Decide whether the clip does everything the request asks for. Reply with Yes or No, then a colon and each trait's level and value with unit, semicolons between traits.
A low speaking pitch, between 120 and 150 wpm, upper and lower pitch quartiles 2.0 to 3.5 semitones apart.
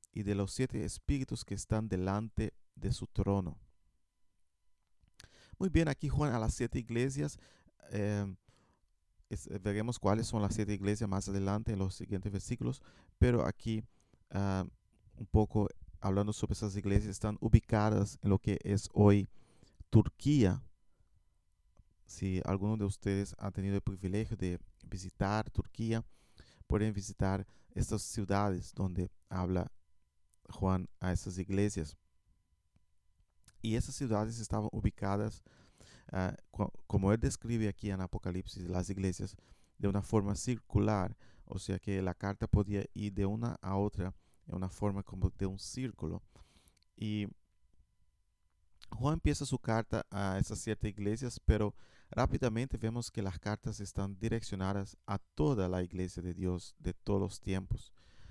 Yes: low, 100 Hz; average, 140 wpm; average, 2.9 semitones